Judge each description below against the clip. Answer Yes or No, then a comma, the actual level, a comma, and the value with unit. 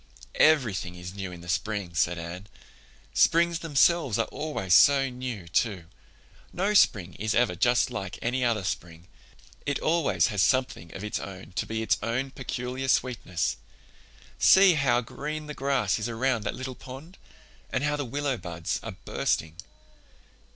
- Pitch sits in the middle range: No, low, 120 Hz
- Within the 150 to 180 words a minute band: Yes, average, 160 wpm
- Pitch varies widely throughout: Yes, wide, 6.6 semitones